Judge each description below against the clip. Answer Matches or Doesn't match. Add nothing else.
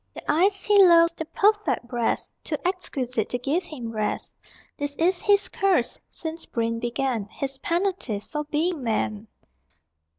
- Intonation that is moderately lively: Doesn't match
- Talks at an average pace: Matches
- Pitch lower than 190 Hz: Doesn't match